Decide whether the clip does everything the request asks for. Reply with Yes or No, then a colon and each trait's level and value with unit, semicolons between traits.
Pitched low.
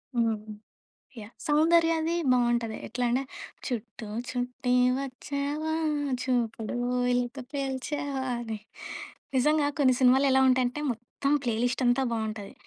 No: very high, 255 Hz